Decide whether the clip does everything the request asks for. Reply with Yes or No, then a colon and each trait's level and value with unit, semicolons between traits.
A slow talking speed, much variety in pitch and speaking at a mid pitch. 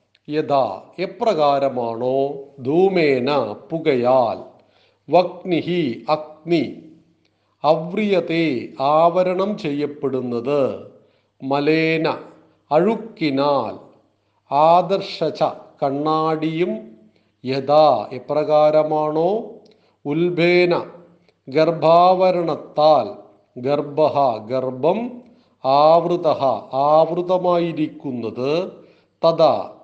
No: slow, 45 wpm; average, 3.7 semitones; medium, 155 Hz